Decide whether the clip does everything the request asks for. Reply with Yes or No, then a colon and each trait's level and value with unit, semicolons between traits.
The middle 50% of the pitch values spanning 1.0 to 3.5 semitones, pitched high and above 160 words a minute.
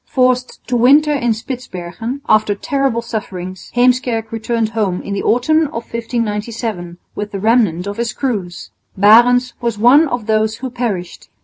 No: average, 3.1 semitones; high, 230 Hz; average, 150 wpm